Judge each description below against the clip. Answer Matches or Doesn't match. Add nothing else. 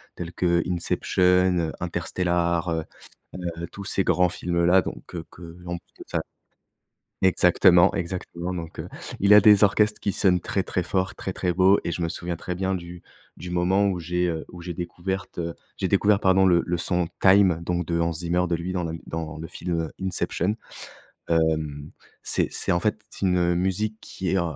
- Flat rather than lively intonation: Matches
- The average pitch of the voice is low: Matches